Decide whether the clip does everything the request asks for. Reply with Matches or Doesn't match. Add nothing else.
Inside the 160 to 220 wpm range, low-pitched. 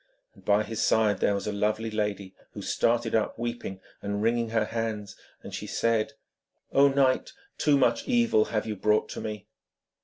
Matches